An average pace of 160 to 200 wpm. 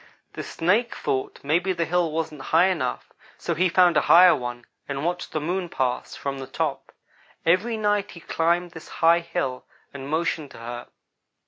Yes: average, 180 wpm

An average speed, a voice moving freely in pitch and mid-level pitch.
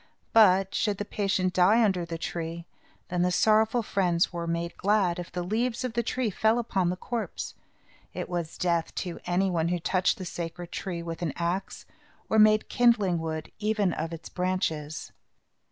No: average, 180 wpm; average, 3.8 semitones; medium, 180 Hz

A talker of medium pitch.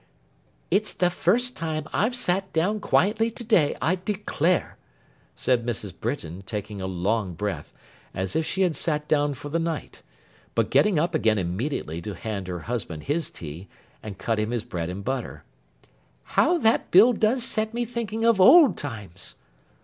Yes: medium, 150 Hz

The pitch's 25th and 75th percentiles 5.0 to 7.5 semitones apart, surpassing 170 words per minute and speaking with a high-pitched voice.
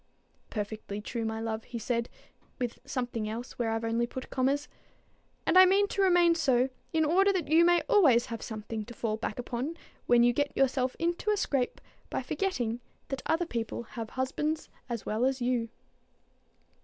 Yes: wide, 5.6 semitones; average, 180 wpm; very high, 250 Hz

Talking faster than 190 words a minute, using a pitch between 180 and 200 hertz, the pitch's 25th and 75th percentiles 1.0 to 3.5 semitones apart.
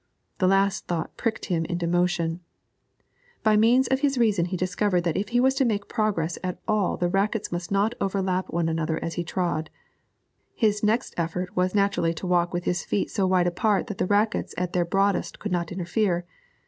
Yes: average, 200 wpm; medium, 185 Hz; average, 3.2 semitones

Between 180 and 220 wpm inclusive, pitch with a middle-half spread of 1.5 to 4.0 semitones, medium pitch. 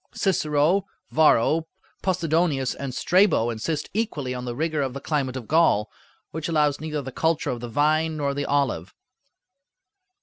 No: average, 155 wpm; average, 3.6 semitones; medium, 150 Hz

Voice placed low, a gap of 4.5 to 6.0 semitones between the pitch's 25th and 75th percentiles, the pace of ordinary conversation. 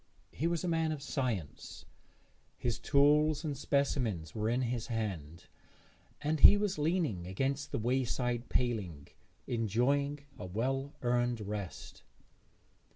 No: low, 125 Hz; average, 4.9 semitones; slow, 125 wpm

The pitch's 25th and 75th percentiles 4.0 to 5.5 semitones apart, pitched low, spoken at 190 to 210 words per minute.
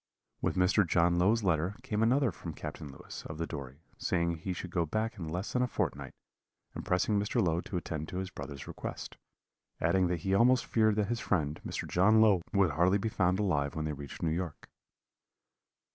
Yes: average, 4.6 semitones; very low, 90 Hz; fast, 205 wpm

